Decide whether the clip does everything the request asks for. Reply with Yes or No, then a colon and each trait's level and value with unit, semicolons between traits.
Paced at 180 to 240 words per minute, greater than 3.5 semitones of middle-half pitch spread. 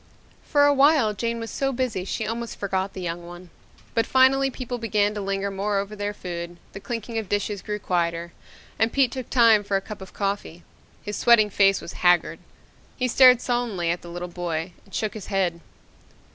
Yes: average, 200 wpm; average, 4.2 semitones